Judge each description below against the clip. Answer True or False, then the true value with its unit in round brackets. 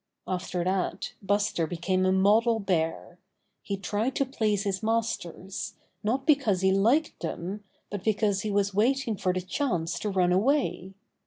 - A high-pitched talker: True (200 Hz)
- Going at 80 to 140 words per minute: False (155 wpm)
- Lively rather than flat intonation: False (3.2 semitones)